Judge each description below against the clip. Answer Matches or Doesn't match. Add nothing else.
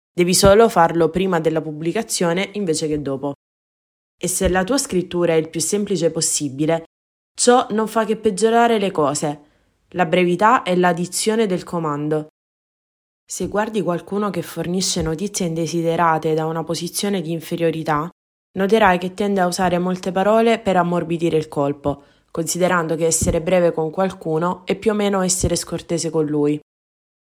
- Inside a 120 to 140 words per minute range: Doesn't match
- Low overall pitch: Doesn't match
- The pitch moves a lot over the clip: Doesn't match